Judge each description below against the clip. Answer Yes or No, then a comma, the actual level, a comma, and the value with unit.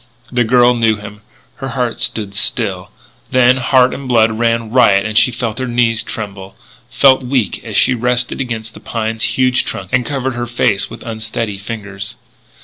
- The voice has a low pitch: Yes, low, 115 Hz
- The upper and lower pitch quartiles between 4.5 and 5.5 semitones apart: No, narrow, 2.5 semitones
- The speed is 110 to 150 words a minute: No, average, 175 wpm